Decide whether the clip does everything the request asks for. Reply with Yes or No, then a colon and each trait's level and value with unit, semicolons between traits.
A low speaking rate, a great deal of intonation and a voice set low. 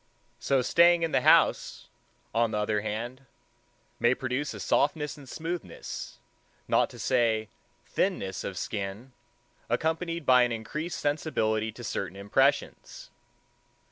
Yes: slow, 125 wpm; wide, 5.8 semitones; low, 125 Hz